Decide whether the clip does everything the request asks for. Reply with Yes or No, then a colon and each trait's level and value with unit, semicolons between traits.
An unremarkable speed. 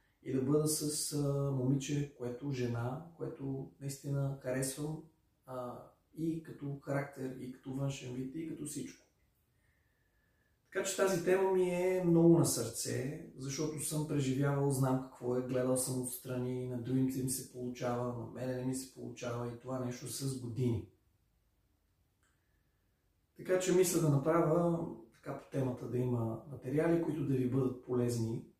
Yes: average, 150 wpm